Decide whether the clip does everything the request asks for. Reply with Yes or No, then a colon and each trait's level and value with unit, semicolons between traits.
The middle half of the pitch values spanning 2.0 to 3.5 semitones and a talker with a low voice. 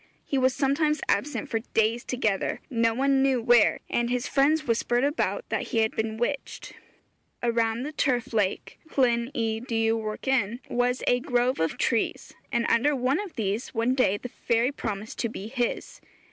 No: average, 2.9 semitones; high, 240 Hz